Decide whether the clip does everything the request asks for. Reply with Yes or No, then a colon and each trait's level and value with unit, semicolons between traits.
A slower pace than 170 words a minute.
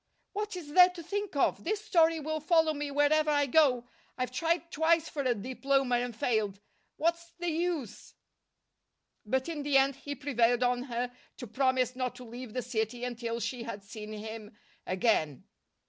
No: average, 175 wpm